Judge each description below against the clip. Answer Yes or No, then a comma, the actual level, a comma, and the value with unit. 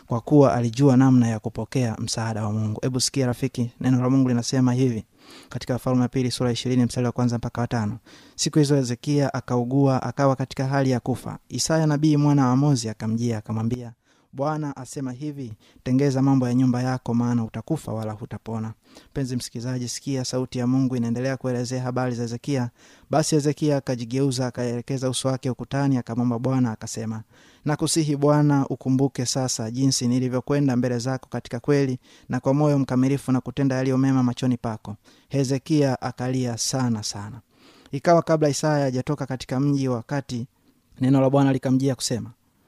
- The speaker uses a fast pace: Yes, fast, 150 wpm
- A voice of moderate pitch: No, low, 130 Hz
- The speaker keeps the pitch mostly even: Yes, narrow, 2.2 semitones